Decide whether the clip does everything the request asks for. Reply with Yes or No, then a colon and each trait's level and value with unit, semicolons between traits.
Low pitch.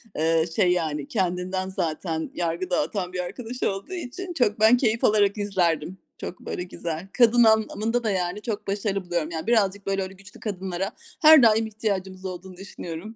No: high, 195 Hz